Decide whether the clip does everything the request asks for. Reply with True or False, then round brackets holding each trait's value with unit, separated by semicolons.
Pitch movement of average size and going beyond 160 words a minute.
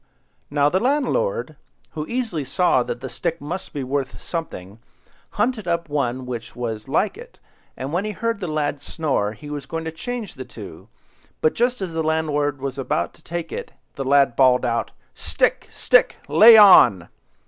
False (6.7 semitones; 175 wpm)